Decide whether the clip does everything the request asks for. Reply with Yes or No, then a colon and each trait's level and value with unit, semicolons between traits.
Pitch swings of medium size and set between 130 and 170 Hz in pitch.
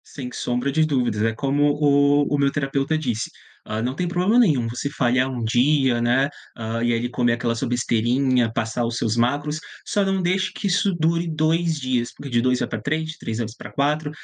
Yes: average, 4.4 semitones; low, 135 Hz